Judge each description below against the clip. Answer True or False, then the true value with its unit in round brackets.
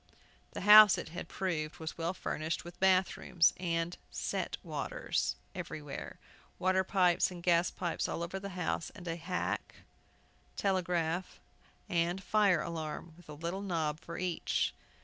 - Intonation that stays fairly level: True (2.0 semitones)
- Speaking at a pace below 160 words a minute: True (150 wpm)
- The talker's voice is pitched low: False (175 Hz)